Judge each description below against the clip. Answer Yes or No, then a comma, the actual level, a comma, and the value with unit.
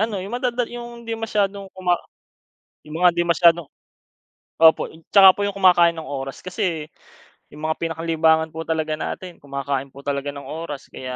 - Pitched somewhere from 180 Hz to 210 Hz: No, medium, 165 Hz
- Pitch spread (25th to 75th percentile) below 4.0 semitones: No, average, 4.4 semitones